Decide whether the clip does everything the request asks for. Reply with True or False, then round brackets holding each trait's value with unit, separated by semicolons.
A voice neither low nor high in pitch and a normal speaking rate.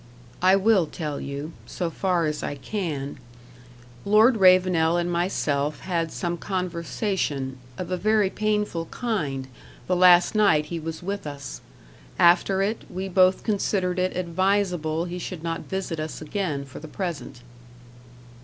True (175 Hz; 145 wpm)